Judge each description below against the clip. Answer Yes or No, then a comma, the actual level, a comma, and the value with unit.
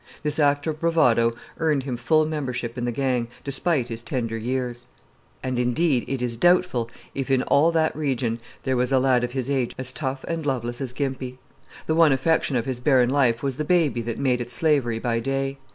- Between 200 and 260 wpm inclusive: Yes, fast, 205 wpm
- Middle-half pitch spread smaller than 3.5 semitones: Yes, average, 3.1 semitones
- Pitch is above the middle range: No, low, 130 Hz